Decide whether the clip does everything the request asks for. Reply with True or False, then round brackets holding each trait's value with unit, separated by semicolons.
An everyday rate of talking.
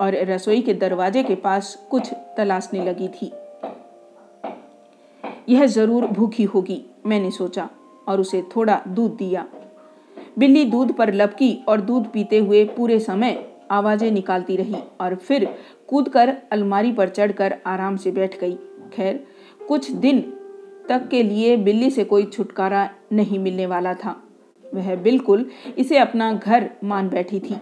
True (145 wpm)